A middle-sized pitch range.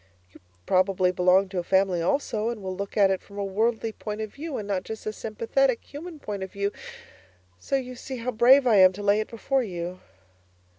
Yes: average, 3.9 semitones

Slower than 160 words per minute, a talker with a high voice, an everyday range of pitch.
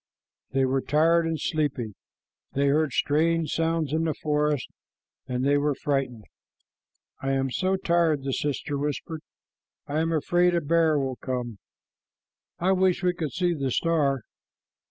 No: average, 150 wpm; medium, 150 Hz; average, 3.4 semitones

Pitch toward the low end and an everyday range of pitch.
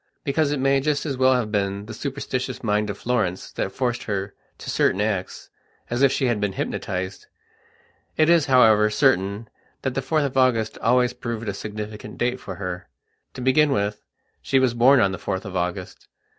Yes: low, 115 Hz; average, 4.5 semitones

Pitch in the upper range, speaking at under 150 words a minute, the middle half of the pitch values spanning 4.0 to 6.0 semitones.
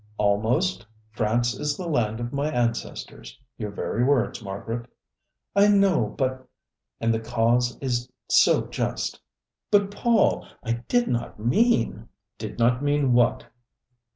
No: low, 120 Hz; average, 140 wpm; average, 4.5 semitones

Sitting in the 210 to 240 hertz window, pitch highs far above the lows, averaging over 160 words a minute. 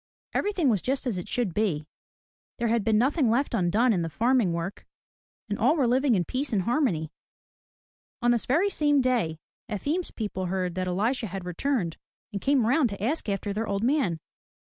Yes: high, 225 Hz; wide, 5.8 semitones; average, 190 wpm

